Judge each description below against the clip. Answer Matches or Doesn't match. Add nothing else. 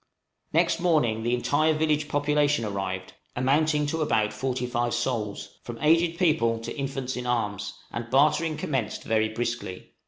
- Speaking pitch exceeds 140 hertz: Doesn't match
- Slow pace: Doesn't match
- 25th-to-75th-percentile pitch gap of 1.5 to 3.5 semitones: Doesn't match